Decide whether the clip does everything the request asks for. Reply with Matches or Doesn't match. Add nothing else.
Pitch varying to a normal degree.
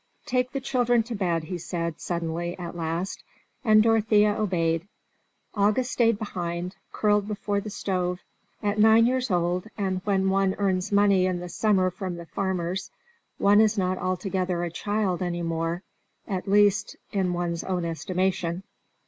Matches